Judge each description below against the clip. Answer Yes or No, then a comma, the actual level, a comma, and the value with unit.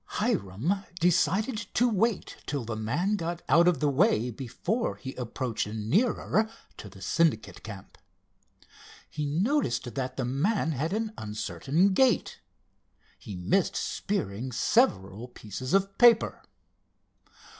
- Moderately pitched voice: Yes, medium, 150 Hz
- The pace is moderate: No, slow, 125 wpm